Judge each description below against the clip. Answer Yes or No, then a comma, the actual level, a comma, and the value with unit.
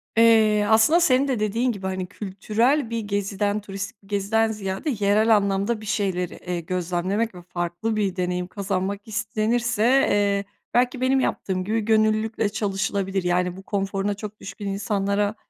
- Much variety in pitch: No, narrow, 2.4 semitones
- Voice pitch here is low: No, high, 205 Hz